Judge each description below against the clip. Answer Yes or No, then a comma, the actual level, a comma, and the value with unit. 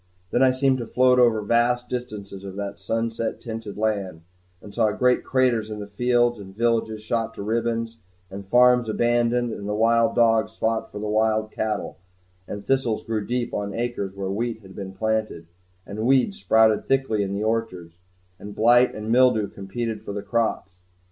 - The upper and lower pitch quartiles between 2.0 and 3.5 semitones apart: Yes, narrow, 2.6 semitones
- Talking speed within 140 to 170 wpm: No, average, 180 wpm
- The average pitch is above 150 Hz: No, low, 110 Hz